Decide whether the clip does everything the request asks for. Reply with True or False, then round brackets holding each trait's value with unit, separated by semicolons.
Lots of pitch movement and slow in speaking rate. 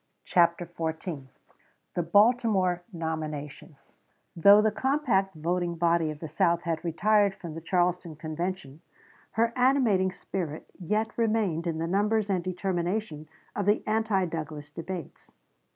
False (4.0 semitones; 130 wpm)